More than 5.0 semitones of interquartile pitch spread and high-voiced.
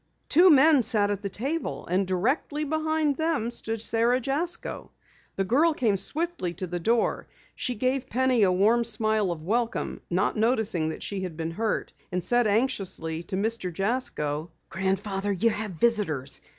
Yes: wide, 5.4 semitones; high, 220 Hz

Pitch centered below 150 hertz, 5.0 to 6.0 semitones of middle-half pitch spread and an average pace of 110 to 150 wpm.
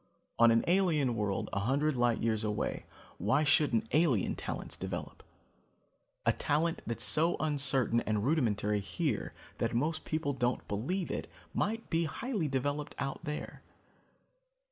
Yes: medium, 140 Hz; wide, 5.4 semitones; average, 140 wpm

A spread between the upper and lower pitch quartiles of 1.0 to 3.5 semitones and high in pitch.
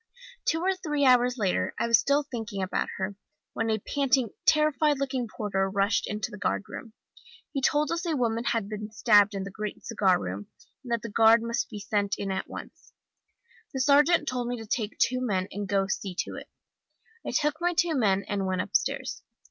No: average, 5.2 semitones; high, 225 Hz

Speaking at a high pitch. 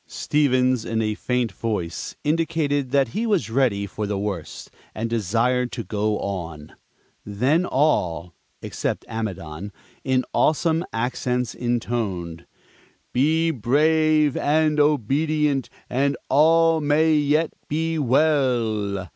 No: low, 125 Hz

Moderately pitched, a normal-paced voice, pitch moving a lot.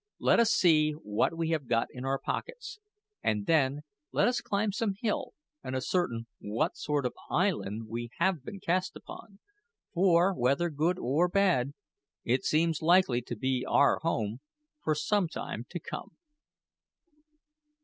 Yes: medium, 155 Hz; average, 150 wpm; wide, 6.5 semitones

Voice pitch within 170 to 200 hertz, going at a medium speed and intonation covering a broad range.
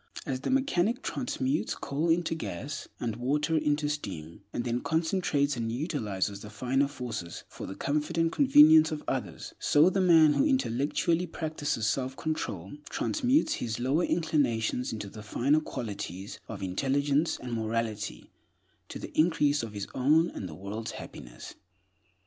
No: medium, 140 Hz; average, 150 wpm; wide, 6.0 semitones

